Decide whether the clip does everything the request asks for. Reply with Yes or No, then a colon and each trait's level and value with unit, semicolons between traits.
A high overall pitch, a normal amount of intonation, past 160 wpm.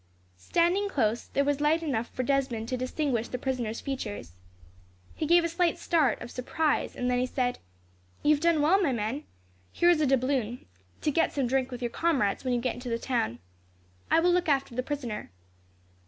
Yes: very high, 265 Hz; average, 4.2 semitones; average, 195 wpm